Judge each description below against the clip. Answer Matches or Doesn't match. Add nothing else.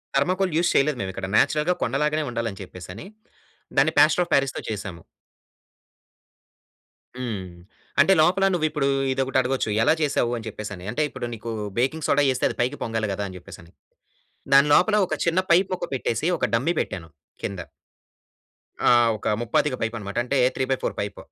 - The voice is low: Matches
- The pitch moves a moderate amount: Doesn't match